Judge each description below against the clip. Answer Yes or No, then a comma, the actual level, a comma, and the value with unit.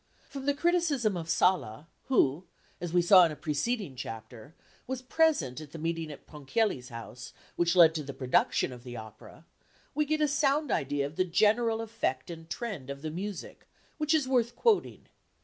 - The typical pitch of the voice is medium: Yes, medium, 175 Hz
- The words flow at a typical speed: Yes, average, 185 wpm